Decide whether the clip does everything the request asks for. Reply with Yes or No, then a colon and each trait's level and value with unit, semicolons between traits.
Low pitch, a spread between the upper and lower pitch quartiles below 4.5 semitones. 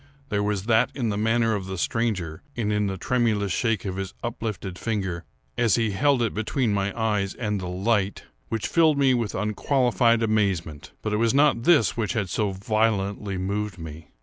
Yes: low, 105 Hz; average, 3.0 semitones